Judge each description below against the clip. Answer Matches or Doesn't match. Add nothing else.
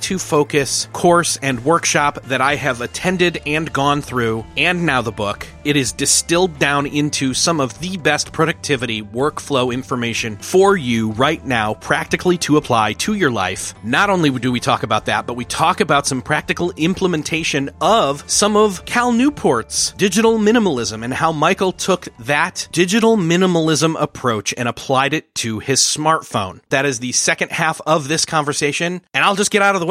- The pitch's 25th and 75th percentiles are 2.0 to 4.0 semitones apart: Doesn't match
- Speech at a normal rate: Matches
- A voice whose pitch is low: Doesn't match